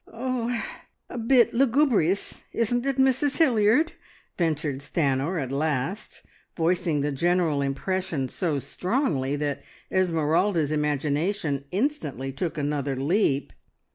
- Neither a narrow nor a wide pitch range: No, wide, 7.8 semitones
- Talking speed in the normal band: No, slow, 110 wpm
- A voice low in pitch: No, medium, 165 Hz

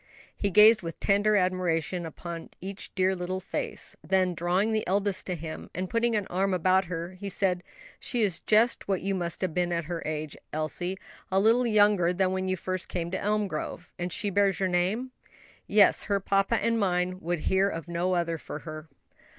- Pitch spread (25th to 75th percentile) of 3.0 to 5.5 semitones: No, narrow, 2.4 semitones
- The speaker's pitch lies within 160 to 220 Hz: Yes, medium, 185 Hz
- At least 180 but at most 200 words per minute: Yes, average, 190 wpm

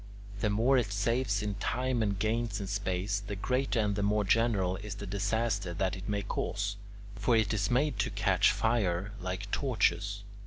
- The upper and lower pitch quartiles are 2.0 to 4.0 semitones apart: Yes, narrow, 2.4 semitones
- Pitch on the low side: Yes, low, 105 Hz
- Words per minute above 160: Yes, average, 185 wpm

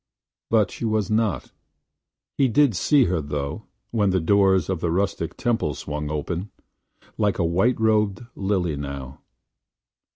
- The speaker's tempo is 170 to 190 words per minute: No, average, 155 wpm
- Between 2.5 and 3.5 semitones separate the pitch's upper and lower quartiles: No, average, 5.1 semitones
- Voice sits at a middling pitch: No, very low, 95 Hz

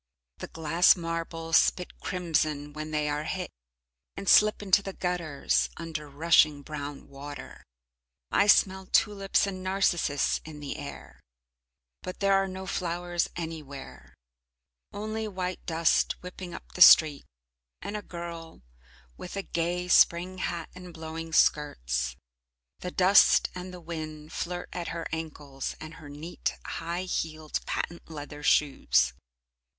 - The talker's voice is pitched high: No, medium, 165 Hz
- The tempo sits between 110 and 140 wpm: Yes, slow, 135 wpm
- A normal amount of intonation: Yes, average, 3.1 semitones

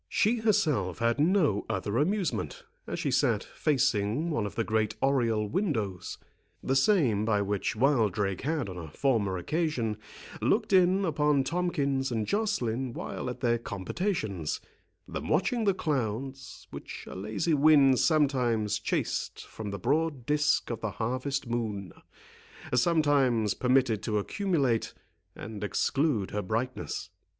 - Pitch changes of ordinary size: No, wide, 6.2 semitones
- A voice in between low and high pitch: No, low, 130 Hz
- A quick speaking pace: No, slow, 135 wpm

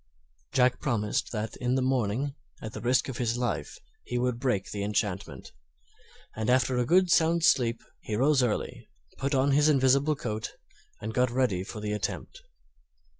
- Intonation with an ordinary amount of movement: Yes, average, 3.6 semitones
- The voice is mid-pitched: No, low, 125 Hz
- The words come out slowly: No, average, 165 wpm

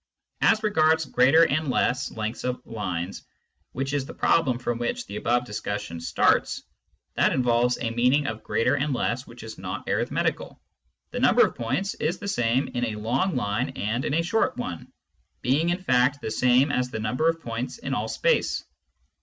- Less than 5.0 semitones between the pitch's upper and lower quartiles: No, average, 5.3 semitones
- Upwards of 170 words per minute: Yes, average, 185 wpm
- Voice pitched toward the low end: Yes, low, 125 Hz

